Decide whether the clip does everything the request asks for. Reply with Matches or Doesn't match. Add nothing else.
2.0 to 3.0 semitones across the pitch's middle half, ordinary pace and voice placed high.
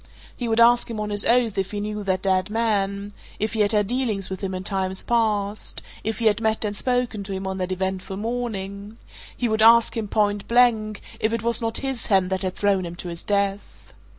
Doesn't match